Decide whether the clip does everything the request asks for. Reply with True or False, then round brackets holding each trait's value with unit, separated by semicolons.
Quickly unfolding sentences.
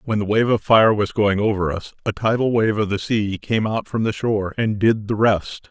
True (255 wpm)